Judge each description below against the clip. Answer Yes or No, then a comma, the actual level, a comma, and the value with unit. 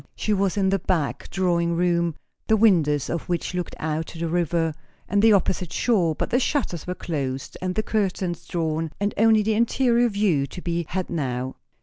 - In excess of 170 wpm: Yes, average, 195 wpm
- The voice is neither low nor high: Yes, medium, 180 Hz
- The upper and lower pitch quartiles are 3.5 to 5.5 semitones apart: Yes, average, 3.8 semitones